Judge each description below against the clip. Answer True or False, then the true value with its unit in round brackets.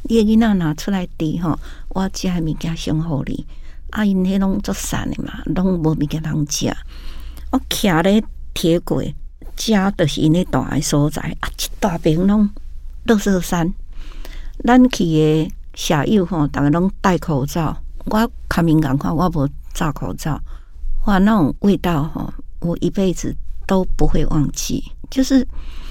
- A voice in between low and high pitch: True (165 Hz)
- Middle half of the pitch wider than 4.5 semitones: True (4.9 semitones)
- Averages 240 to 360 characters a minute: False (210 characters per minute)